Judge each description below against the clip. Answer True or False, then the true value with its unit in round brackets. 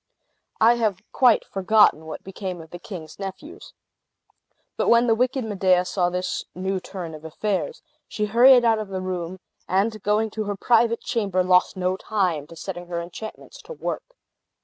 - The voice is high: True (195 Hz)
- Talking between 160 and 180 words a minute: True (170 wpm)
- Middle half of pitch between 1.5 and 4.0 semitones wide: True (3.5 semitones)